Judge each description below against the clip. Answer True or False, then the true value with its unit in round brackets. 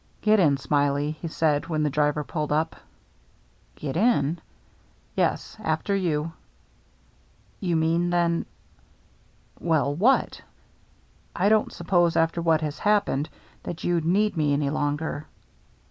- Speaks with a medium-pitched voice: True (160 Hz)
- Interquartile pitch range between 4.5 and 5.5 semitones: False (2.8 semitones)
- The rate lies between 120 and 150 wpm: True (145 wpm)